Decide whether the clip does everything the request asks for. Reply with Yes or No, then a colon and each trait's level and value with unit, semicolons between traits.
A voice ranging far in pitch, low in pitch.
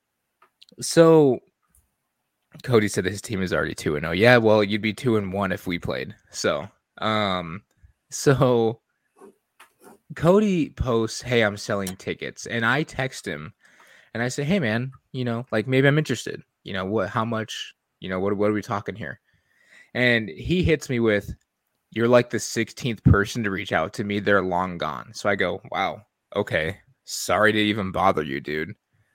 No: average, 3.7 semitones; low, 110 Hz